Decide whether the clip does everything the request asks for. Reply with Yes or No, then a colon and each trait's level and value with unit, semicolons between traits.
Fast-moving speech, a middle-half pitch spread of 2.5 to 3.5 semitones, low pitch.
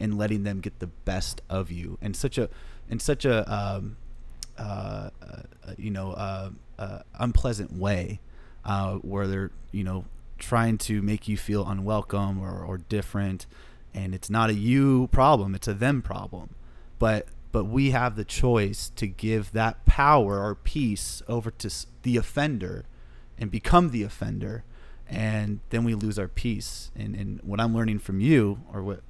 No: average, 170 wpm; average, 2.9 semitones; low, 105 Hz